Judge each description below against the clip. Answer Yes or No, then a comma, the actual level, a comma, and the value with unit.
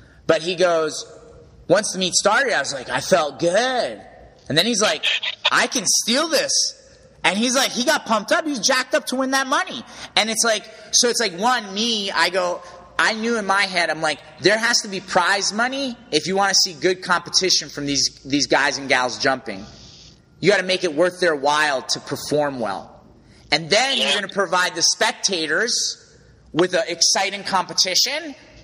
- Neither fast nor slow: Yes, average, 195 wpm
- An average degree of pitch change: No, wide, 6.2 semitones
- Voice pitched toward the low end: No, high, 190 Hz